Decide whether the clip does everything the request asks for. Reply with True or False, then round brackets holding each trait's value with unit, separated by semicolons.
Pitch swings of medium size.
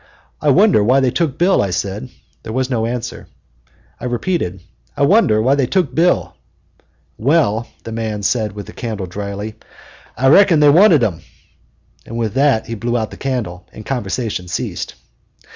True (4.6 semitones)